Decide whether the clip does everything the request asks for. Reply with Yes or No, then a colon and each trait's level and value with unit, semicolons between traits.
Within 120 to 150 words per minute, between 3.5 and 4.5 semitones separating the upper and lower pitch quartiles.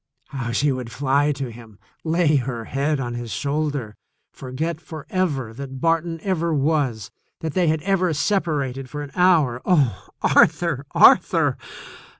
Yes: average, 145 wpm; average, 4.1 semitones